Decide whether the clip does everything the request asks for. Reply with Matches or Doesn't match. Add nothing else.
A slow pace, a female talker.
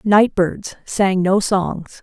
Matches